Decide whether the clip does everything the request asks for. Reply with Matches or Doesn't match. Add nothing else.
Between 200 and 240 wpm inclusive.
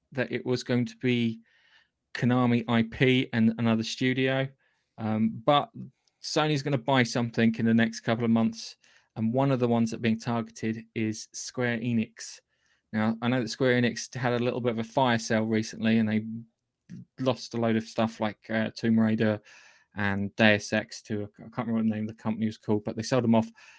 Matches